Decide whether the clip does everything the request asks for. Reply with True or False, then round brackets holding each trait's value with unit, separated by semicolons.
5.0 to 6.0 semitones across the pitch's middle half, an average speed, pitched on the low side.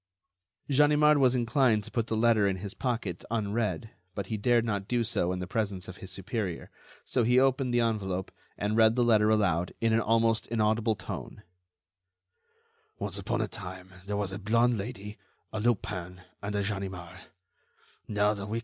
False (3.3 semitones; 165 wpm; 110 Hz)